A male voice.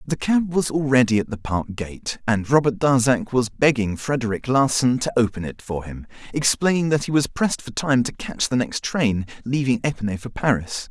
Yes: male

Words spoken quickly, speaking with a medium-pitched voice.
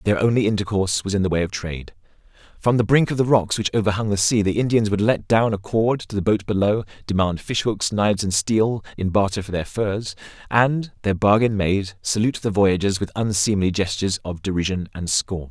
No: fast, 215 wpm; low, 100 Hz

